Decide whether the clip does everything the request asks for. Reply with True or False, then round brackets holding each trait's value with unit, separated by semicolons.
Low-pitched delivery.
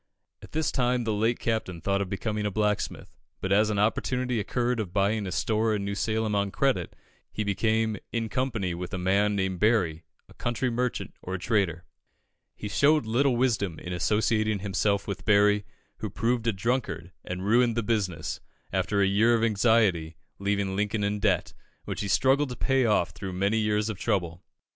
True (105 Hz)